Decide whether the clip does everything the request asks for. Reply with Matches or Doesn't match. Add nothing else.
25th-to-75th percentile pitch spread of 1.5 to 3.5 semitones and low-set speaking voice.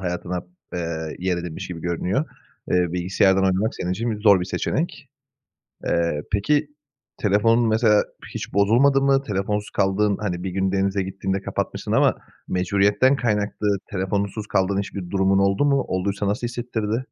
Matches